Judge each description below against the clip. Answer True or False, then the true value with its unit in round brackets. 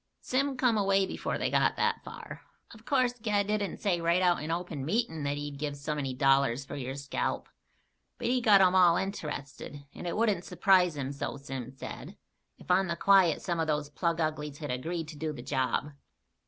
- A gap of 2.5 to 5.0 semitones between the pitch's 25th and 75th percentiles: False (5.5 semitones)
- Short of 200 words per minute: False (205 wpm)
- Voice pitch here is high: False (165 Hz)